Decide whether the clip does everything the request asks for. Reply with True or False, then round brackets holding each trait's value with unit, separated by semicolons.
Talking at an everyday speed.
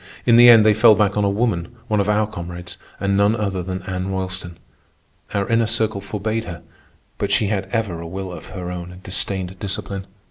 False (210 wpm)